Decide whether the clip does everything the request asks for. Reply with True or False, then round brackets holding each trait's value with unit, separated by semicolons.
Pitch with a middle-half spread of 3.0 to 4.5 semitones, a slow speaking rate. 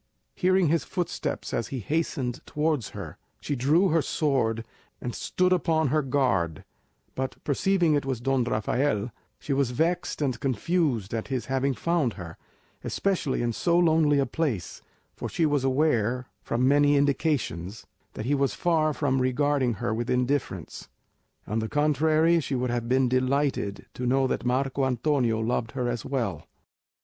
False (4.0 semitones; 160 wpm)